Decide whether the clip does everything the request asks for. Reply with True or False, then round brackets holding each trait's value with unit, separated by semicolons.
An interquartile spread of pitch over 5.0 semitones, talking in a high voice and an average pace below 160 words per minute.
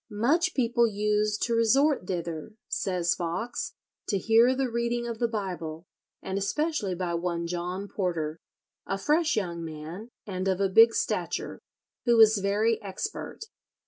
False (4.7 semitones; 205 Hz; 145 wpm)